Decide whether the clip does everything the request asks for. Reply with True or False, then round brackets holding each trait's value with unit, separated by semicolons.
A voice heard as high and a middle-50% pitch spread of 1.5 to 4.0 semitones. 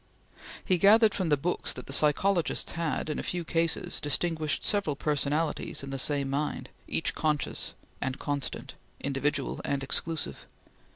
False (150 Hz; 3.1 semitones)